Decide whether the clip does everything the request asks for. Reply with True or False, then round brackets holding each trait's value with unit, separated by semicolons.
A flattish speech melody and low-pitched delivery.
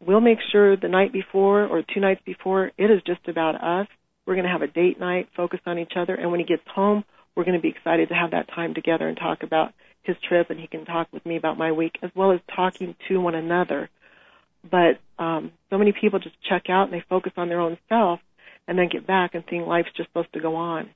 False (2.2 semitones; 180 Hz)